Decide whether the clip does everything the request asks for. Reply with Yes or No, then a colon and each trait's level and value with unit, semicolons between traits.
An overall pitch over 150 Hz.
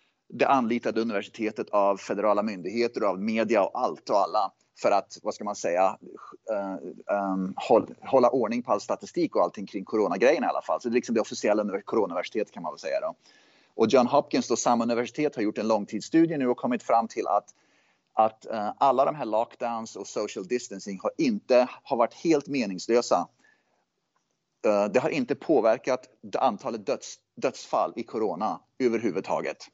No: low, 115 Hz